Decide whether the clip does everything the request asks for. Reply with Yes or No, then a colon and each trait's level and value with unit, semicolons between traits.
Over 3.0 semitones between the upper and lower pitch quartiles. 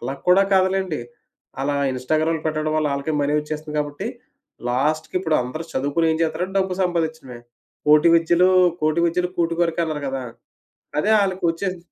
No: narrow, 2.6 semitones